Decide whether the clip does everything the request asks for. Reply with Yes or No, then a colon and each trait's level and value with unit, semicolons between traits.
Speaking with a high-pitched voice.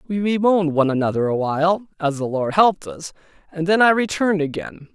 No: medium, 170 Hz